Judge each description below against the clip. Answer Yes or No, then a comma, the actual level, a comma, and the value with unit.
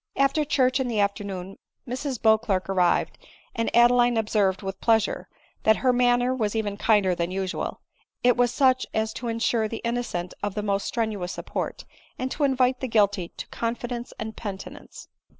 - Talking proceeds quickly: No, average, 170 wpm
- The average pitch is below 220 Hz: No, high, 225 Hz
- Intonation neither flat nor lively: Yes, average, 3.4 semitones